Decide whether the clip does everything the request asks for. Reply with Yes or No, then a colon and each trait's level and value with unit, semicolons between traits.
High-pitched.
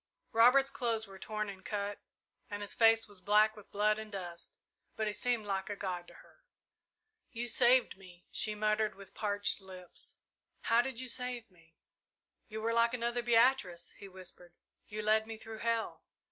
Yes: high, 215 Hz